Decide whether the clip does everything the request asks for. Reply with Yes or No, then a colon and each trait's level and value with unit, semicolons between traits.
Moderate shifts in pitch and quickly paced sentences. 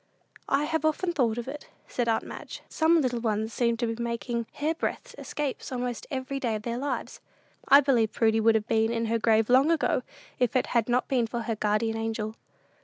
Yes: average, 3.2 semitones; fast, 210 wpm